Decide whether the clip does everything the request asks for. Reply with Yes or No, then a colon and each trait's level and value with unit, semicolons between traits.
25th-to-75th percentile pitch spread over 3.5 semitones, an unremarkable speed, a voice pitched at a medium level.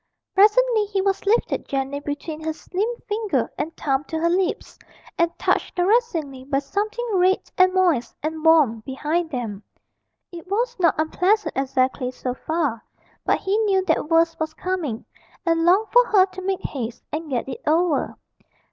No: average, 5.3 semitones; average, 165 wpm; very high, 330 Hz